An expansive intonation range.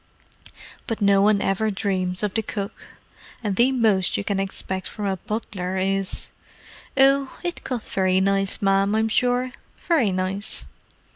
No: narrow, 2.6 semitones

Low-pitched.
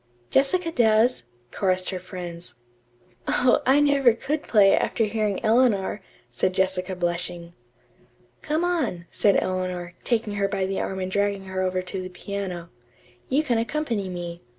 No: high, 195 Hz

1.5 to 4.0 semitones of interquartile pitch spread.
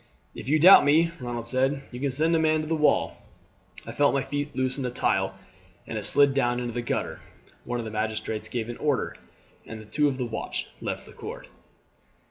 Yes: average, 3.5 semitones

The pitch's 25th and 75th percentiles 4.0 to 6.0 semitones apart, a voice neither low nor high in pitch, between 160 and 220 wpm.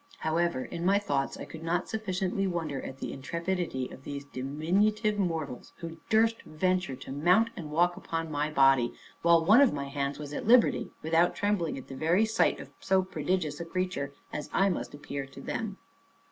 Yes: average, 4.7 semitones; medium, 165 Hz; average, 190 wpm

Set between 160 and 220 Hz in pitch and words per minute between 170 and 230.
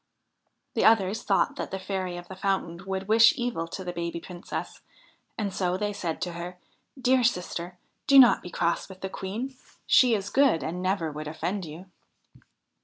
Yes: high, 190 Hz; average, 180 wpm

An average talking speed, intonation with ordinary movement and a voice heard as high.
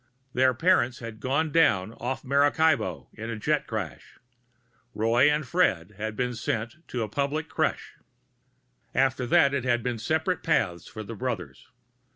No: average, 155 wpm; average, 4.7 semitones; low, 125 Hz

